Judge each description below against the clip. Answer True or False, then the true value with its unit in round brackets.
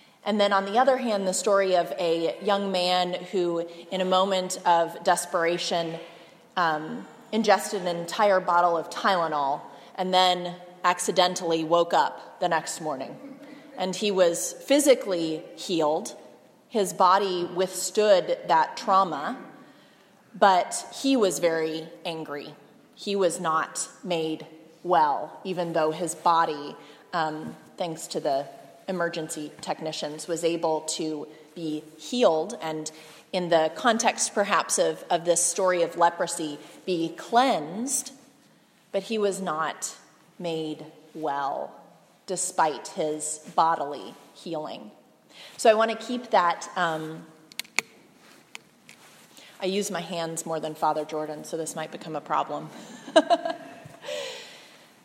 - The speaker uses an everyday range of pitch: True (3.6 semitones)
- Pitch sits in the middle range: True (175 Hz)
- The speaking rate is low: True (120 wpm)